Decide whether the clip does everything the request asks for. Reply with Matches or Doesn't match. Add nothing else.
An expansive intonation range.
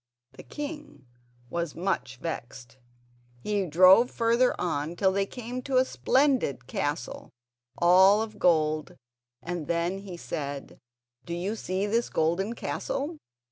Matches